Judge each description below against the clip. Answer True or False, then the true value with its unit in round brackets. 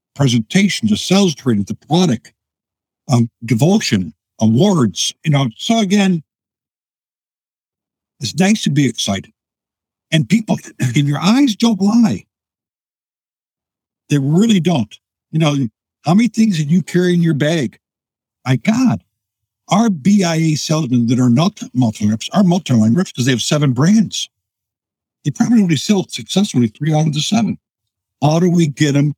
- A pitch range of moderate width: False (8.4 semitones)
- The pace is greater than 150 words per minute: False (145 wpm)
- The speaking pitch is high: False (150 Hz)